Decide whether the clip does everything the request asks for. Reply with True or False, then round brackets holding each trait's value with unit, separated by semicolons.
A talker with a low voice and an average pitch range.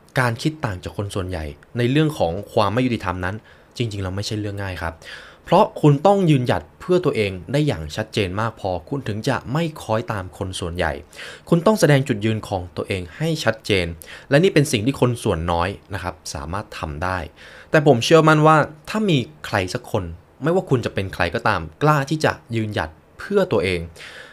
False (110 Hz; 7.6 semitones)